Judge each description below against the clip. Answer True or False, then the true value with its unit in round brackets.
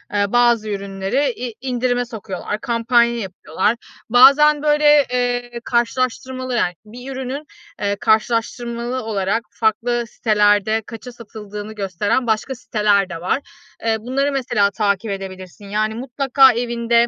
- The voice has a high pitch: True (235 Hz)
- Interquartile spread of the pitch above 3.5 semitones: False (3.1 semitones)